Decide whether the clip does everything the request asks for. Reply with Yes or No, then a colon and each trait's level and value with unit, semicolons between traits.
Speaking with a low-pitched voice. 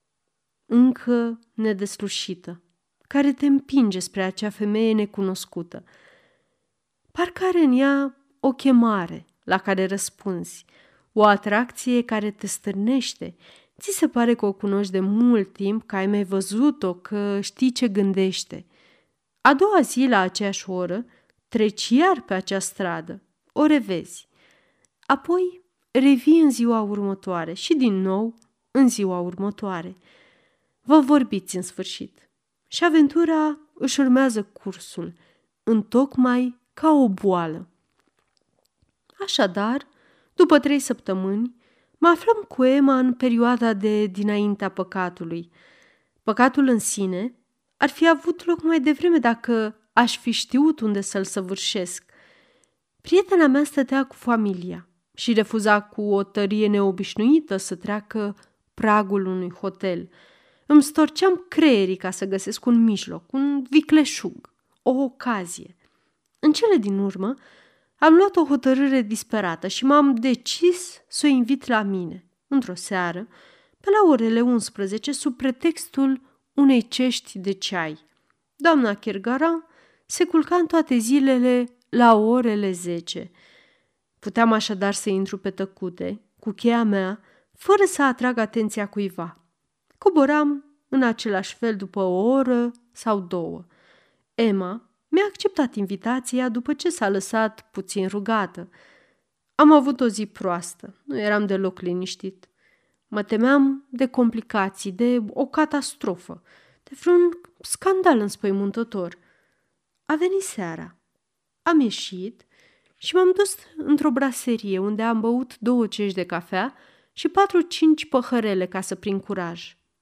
No: high, 230 Hz